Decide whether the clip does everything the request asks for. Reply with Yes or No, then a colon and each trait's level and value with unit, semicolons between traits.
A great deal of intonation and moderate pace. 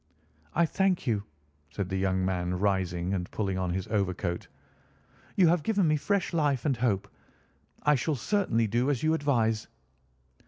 Yes: wide, 8.1 semitones; average, 160 wpm